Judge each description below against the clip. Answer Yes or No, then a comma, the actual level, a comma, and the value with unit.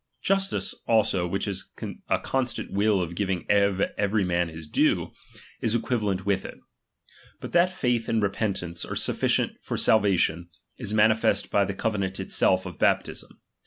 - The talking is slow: No, average, 155 wpm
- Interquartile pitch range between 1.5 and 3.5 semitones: Yes, average, 3.1 semitones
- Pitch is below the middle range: Yes, low, 100 Hz